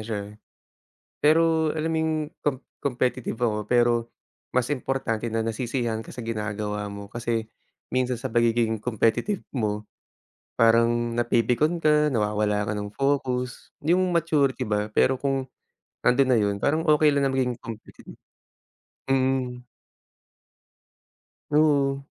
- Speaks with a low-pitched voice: Yes, low, 125 Hz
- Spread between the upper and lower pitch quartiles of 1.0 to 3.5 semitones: No, average, 3.9 semitones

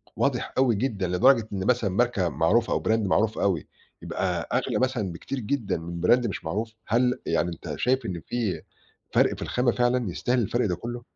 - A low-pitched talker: Yes, low, 110 Hz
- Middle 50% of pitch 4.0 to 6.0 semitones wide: Yes, average, 5.1 semitones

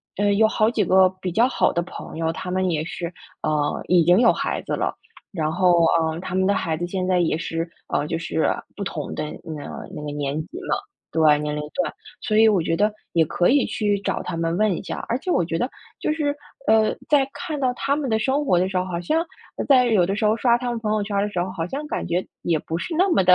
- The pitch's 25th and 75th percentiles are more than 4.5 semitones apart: Yes, average, 5.0 semitones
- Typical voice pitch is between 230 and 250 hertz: No, medium, 185 Hz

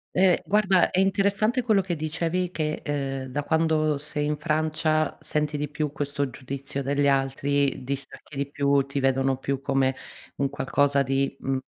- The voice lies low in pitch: No, medium, 145 Hz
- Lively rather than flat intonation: No, narrow, 2.5 semitones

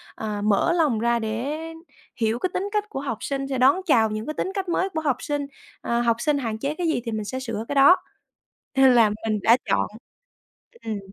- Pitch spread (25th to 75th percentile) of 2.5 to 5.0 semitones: No, wide, 5.5 semitones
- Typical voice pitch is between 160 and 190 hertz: No, very high, 260 Hz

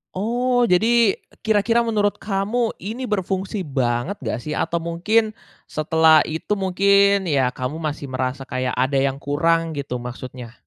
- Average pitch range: No, wide, 7.2 semitones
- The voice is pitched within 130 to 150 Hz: No, medium, 170 Hz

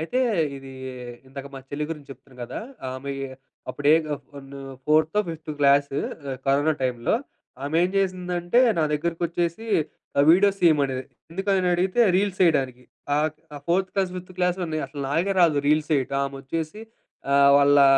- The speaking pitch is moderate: Yes, medium, 155 Hz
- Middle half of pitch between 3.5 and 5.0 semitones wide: Yes, average, 4.3 semitones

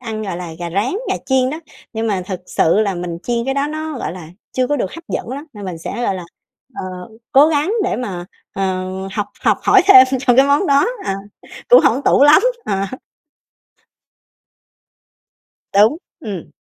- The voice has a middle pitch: No, high, 235 Hz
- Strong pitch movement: Yes, wide, 6.7 semitones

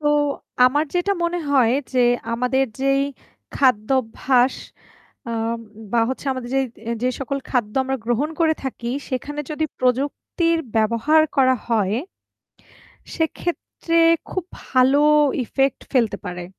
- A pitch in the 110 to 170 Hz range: No, very high, 260 Hz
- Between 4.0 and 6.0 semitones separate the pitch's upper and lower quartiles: No, average, 3.5 semitones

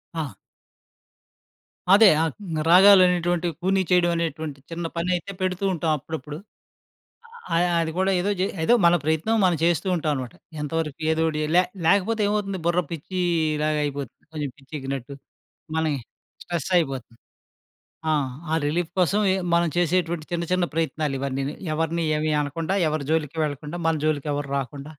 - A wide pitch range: No, average, 3.0 semitones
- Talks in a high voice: No, medium, 165 Hz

